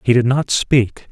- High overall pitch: No, low, 125 Hz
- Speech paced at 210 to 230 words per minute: Yes, fast, 215 wpm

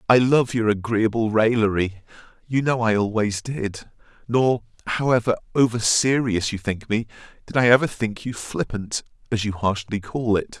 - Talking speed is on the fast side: No, average, 160 wpm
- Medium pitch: No, low, 110 Hz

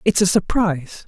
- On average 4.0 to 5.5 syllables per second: Yes, 5.2 syllables/s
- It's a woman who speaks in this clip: Yes, female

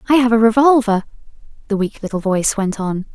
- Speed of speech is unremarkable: Yes, average, 190 wpm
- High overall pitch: Yes, high, 220 Hz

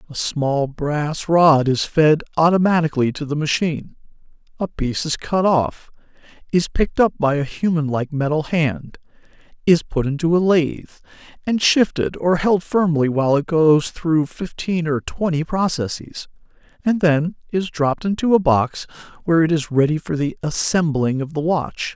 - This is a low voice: No, medium, 160 Hz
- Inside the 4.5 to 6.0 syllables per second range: Yes, 4.7 syllables/s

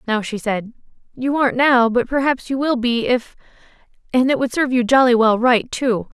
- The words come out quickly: No, average, 195 wpm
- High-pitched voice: Yes, high, 245 Hz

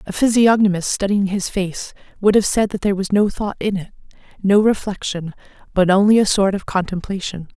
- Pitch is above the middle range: Yes, high, 195 Hz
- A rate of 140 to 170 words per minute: No, average, 180 wpm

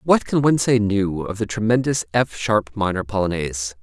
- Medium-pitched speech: No, low, 110 Hz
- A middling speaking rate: Yes, average, 190 wpm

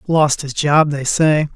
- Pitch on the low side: No, medium, 150 Hz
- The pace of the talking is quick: No, average, 195 wpm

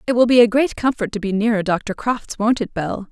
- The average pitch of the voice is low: No, high, 220 Hz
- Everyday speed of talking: No, fast, 270 wpm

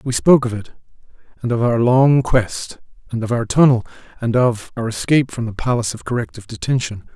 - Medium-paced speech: Yes, average, 195 wpm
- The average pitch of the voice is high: No, low, 120 Hz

